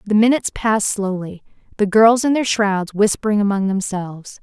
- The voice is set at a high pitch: Yes, high, 205 Hz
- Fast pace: No, average, 165 wpm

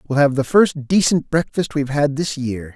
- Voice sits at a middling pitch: Yes, medium, 145 Hz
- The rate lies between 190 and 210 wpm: No, fast, 220 wpm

